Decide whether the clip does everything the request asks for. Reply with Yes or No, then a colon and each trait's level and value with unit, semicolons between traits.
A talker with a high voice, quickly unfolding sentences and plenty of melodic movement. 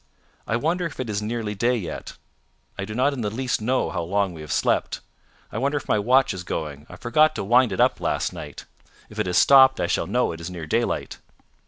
No: low, 110 Hz; fast, 235 wpm; wide, 5.9 semitones